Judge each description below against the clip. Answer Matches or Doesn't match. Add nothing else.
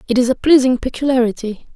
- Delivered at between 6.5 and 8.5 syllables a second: Matches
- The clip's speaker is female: Matches